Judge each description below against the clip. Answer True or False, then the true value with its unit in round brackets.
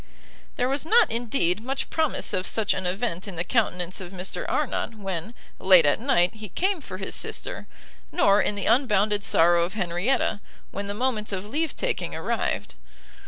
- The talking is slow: False (175 wpm)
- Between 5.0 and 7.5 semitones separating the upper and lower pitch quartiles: True (5.3 semitones)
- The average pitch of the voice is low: False (205 Hz)